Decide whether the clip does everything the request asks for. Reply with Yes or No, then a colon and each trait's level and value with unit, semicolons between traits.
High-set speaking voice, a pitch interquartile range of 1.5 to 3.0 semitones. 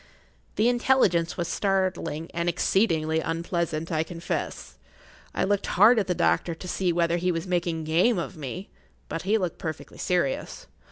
No: medium, 175 Hz; narrow, 2.6 semitones